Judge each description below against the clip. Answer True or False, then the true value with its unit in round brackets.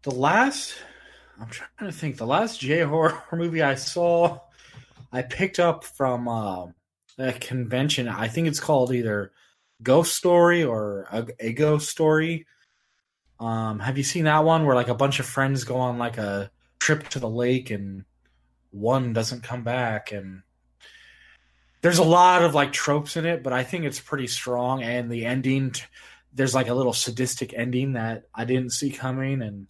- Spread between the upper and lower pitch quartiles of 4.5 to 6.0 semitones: True (4.9 semitones)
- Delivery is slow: False (170 wpm)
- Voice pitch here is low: True (130 Hz)